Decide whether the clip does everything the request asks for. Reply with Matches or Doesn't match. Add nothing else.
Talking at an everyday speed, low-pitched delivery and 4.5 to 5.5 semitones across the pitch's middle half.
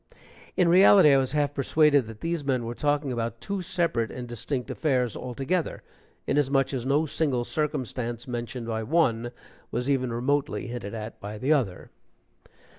Doesn't match